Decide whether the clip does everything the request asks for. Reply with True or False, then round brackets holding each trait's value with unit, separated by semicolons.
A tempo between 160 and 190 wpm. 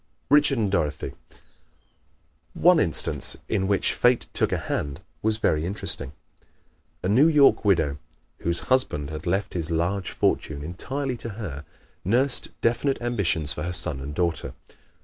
False (150 wpm)